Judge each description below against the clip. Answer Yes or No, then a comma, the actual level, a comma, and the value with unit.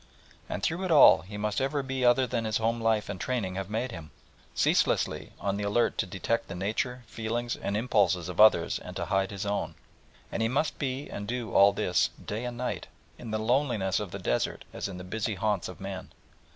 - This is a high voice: No, low, 110 Hz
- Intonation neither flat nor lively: Yes, average, 3.8 semitones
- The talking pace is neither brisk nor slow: No, fast, 215 wpm